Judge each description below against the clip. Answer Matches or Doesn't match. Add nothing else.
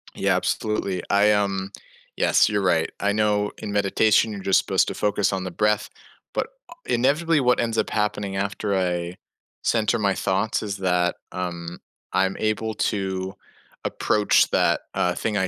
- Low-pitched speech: Matches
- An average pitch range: Doesn't match